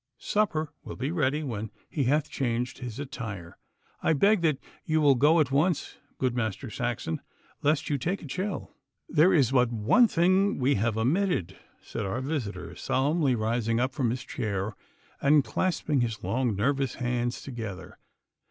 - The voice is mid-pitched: No, low, 130 Hz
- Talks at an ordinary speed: Yes, average, 165 wpm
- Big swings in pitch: No, average, 4.9 semitones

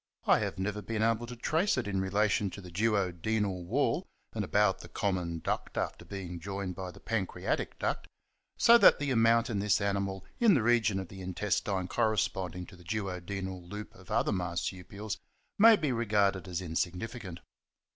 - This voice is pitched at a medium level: No, low, 100 Hz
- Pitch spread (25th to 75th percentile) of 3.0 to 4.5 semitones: Yes, average, 3.4 semitones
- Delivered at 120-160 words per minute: No, average, 185 wpm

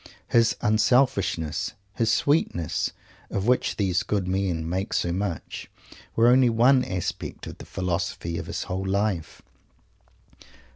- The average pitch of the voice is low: Yes, low, 100 Hz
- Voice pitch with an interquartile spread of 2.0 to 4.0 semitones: No, average, 4.4 semitones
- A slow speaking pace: Yes, slow, 130 wpm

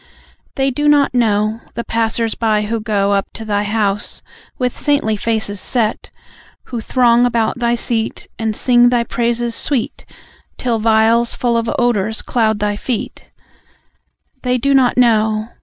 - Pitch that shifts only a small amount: Yes, narrow, 2.0 semitones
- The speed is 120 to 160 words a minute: Yes, average, 150 wpm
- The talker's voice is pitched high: Yes, high, 230 Hz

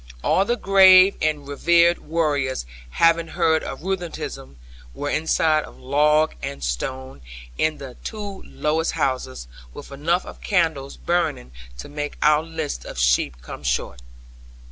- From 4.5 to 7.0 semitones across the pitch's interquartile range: No, average, 4.1 semitones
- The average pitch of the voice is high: No, medium, 155 Hz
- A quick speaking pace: No, average, 140 wpm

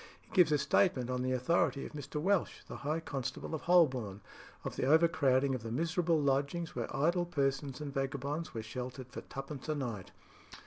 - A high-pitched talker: No, medium, 140 Hz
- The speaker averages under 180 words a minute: No, average, 185 wpm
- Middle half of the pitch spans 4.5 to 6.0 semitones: No, average, 3.8 semitones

